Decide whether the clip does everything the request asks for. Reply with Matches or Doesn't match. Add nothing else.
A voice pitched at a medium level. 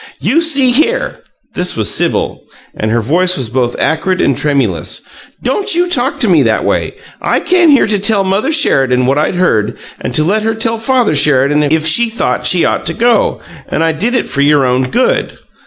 Matches